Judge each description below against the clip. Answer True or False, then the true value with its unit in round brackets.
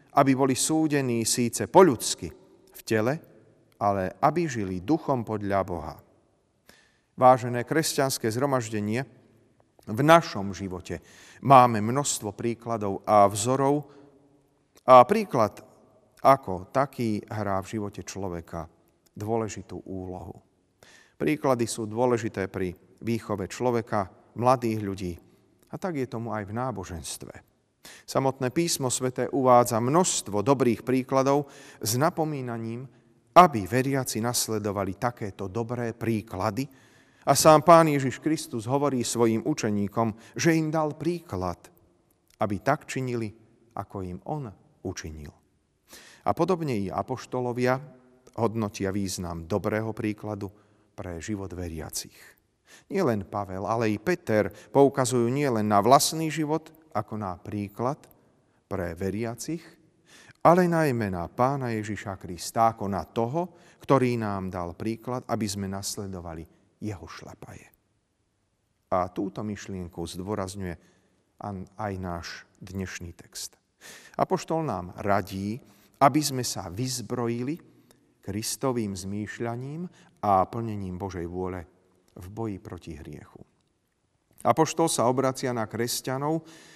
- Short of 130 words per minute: True (110 wpm)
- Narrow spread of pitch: False (4.9 semitones)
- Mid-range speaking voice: False (115 Hz)